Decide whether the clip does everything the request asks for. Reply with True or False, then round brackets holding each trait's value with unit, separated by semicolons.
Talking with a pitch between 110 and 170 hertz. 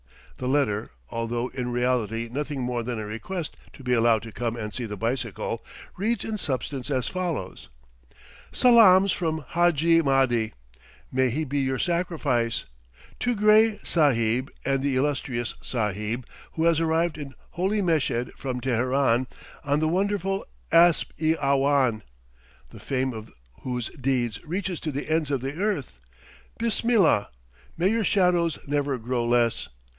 True (135 Hz)